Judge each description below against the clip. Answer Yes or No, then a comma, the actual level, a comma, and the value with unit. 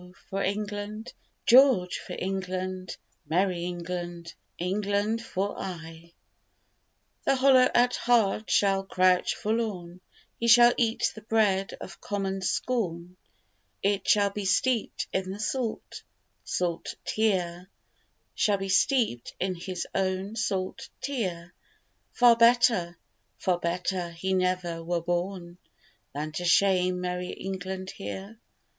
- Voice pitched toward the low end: No, high, 190 Hz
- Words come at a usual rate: No, slow, 115 wpm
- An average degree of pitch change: Yes, average, 3.1 semitones